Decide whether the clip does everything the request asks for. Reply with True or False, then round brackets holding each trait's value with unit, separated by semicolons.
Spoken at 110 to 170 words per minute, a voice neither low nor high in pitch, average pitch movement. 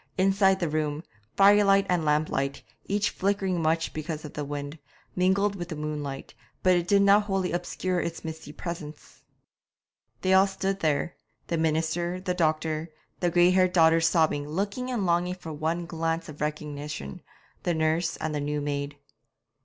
True (160 wpm; 165 Hz; 3.4 semitones)